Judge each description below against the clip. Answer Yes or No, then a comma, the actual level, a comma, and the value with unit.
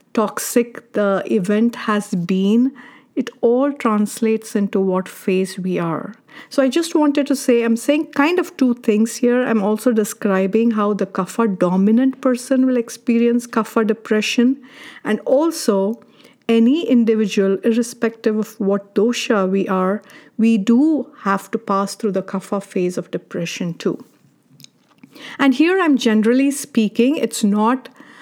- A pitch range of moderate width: Yes, average, 3.7 semitones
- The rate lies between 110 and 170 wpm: Yes, average, 140 wpm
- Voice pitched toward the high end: Yes, high, 225 Hz